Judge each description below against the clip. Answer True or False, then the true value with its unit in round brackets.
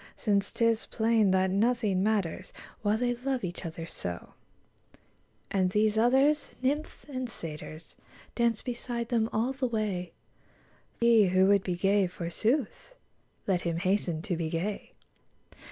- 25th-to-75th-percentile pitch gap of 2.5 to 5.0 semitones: True (4.4 semitones)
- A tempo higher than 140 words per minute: False (135 wpm)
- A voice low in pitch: False (210 Hz)